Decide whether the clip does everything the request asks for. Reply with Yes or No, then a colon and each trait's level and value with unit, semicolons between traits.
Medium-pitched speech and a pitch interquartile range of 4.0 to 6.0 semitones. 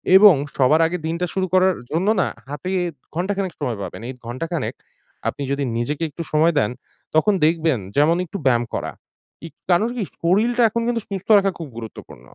Yes: medium, 170 Hz; average, 4.6 semitones